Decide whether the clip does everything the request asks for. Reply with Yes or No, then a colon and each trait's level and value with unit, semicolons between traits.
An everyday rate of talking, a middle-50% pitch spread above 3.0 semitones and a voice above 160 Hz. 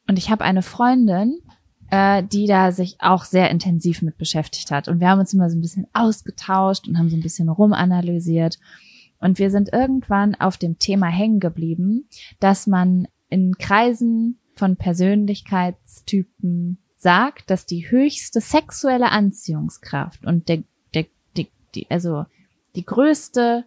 Yes: average, 150 wpm; average, 3.4 semitones; high, 190 Hz